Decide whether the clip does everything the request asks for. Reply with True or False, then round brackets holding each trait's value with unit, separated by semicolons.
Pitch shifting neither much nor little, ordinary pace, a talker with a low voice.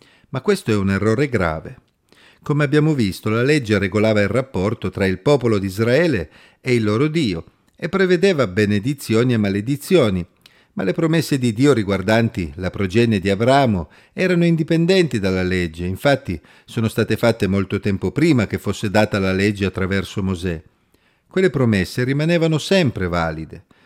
False (6.8 semitones; 155 wpm; 110 Hz)